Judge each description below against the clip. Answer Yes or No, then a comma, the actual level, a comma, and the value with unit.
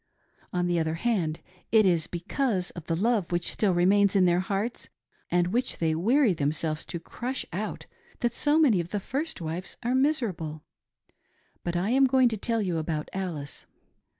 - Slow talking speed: No, average, 175 wpm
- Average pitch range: No, wide, 5.7 semitones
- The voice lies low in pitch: No, medium, 185 Hz